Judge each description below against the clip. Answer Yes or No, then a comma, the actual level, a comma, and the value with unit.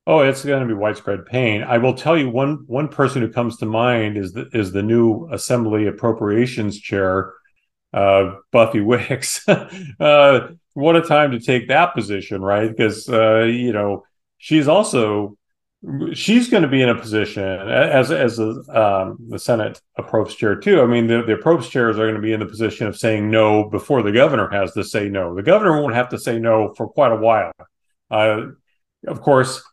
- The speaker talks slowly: No, average, 195 wpm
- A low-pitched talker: Yes, low, 115 Hz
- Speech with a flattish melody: No, average, 4.0 semitones